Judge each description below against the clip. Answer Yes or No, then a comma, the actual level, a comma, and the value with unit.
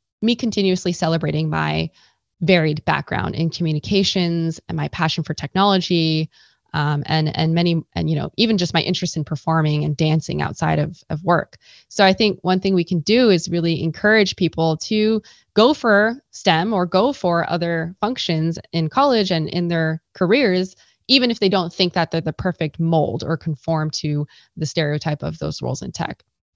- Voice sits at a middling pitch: Yes, medium, 170 Hz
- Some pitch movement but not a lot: Yes, average, 3.2 semitones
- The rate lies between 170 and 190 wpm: Yes, average, 180 wpm